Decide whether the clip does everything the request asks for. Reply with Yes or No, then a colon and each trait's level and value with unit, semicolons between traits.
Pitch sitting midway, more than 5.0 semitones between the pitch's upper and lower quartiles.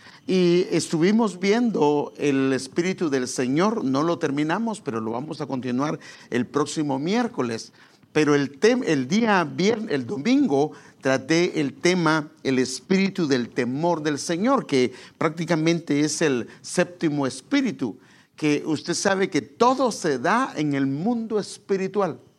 Yes: medium, 160 Hz; wide, 5.6 semitones